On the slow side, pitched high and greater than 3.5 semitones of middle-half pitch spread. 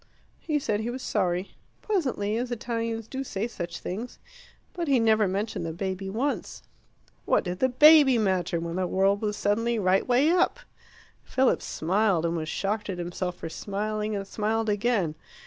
No: average, 170 wpm; high, 210 Hz; average, 4.3 semitones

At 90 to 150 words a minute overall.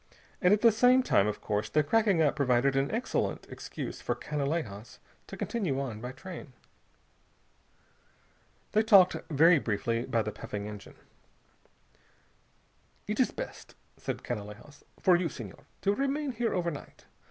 Yes: average, 140 wpm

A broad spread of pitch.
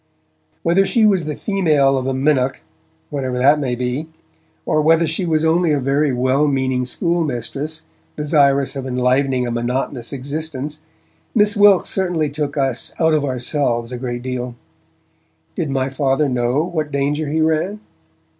No: average, 3.5 semitones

